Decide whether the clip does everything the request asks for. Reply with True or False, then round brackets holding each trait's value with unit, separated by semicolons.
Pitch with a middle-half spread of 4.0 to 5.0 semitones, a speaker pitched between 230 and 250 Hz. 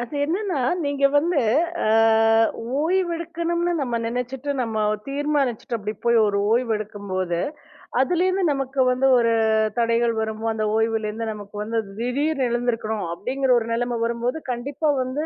True (4.3 semitones; 245 Hz)